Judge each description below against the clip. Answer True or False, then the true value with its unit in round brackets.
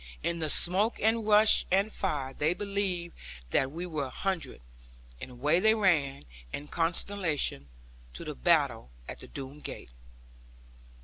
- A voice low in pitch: False (170 Hz)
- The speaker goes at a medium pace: True (145 wpm)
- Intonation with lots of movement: True (5.8 semitones)